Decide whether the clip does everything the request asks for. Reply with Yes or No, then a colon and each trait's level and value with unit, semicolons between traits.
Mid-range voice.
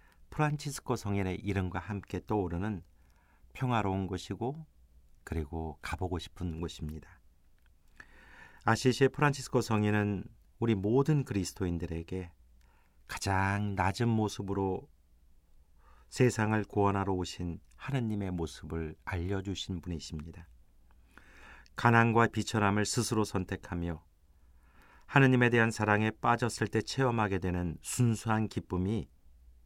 No: very low, 95 Hz